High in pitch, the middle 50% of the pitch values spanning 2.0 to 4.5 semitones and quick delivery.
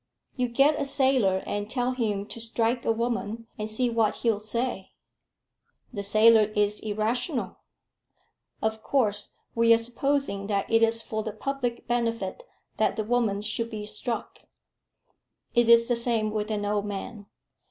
No: high, 225 Hz; narrow, 2.4 semitones; average, 155 wpm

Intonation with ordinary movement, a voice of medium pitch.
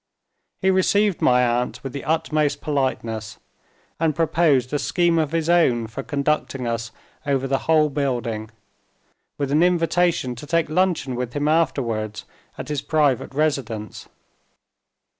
Yes: average, 4.6 semitones; medium, 145 Hz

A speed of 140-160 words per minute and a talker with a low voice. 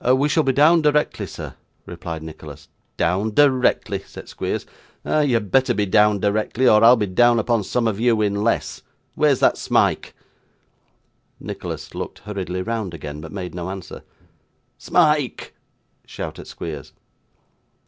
Yes: average, 150 wpm; low, 105 Hz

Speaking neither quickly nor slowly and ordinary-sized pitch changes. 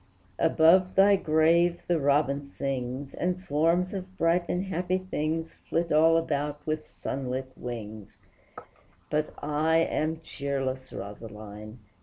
No: slow, 120 wpm; average, 4.0 semitones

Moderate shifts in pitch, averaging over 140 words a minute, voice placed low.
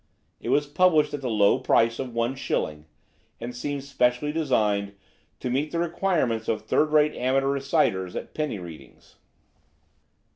Yes: average, 4.6 semitones; average, 150 wpm; low, 130 Hz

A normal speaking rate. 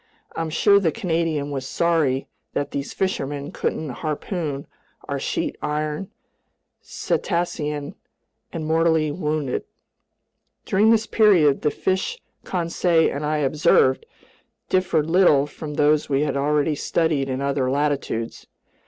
No: slow, 125 wpm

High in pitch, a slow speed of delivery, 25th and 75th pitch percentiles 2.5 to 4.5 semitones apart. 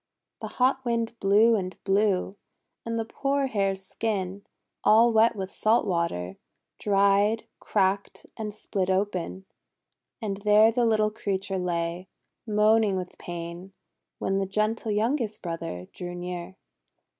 Yes: high, 200 Hz; slow, 130 wpm; average, 2.9 semitones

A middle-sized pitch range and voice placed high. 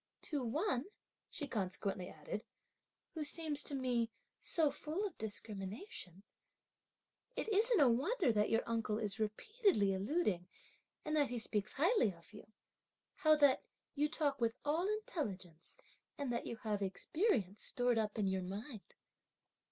No: wide, 6.9 semitones; high, 240 Hz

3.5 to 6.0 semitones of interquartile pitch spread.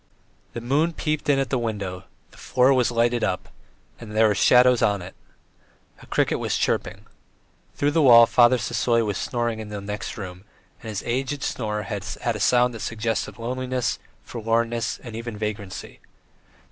No: average, 2.9 semitones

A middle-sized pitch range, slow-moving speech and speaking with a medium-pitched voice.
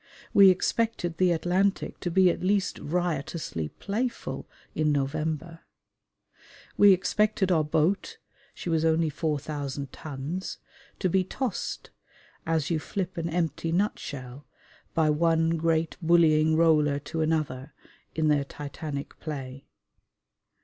Yes: average, 3.0 semitones; slow, 120 wpm; medium, 160 Hz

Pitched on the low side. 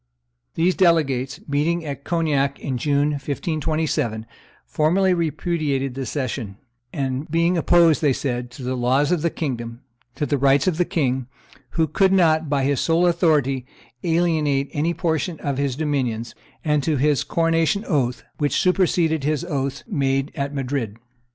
No: medium, 145 Hz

